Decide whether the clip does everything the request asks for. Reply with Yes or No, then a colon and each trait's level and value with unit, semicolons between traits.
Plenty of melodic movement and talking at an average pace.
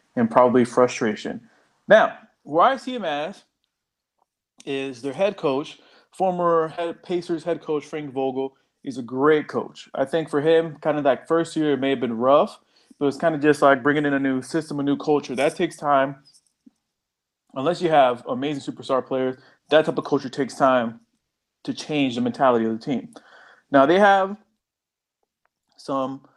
No: average, 3.6 semitones; average, 180 wpm